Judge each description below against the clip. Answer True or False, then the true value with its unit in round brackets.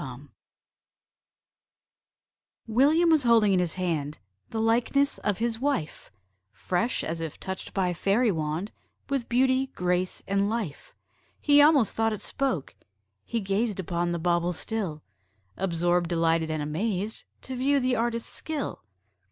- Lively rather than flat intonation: True (5.7 semitones)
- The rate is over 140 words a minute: False (135 wpm)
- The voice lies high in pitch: True (205 Hz)